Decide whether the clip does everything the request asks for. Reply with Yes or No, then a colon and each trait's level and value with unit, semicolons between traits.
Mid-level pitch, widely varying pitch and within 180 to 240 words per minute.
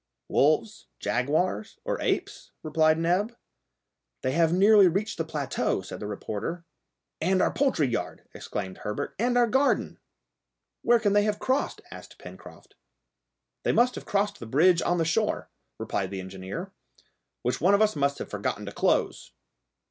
No: medium, 165 Hz; wide, 8.2 semitones; average, 155 wpm